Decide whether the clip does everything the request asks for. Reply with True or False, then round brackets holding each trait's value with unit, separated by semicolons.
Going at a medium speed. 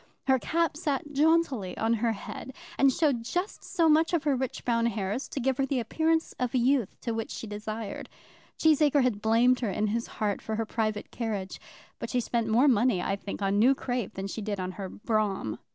False (210 wpm)